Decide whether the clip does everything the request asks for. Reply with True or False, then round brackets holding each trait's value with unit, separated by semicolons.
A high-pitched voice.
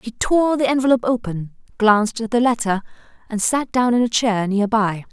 True (230 Hz)